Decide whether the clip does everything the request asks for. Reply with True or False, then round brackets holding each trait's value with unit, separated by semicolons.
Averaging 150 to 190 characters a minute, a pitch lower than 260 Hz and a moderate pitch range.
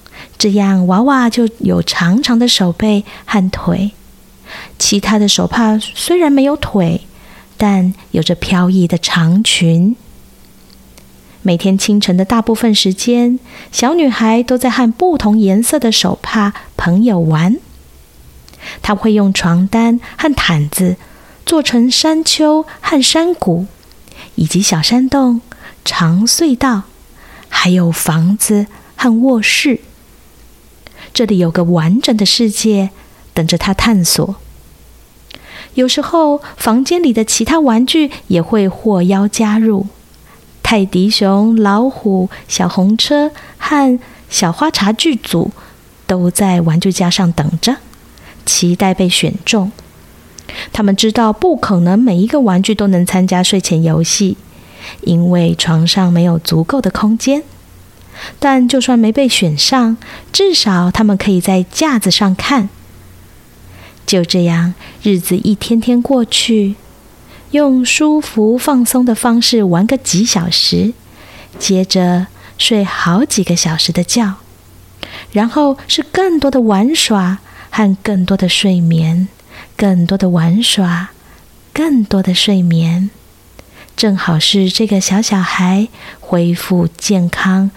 True (180 characters per minute; 200 Hz; 4.8 semitones)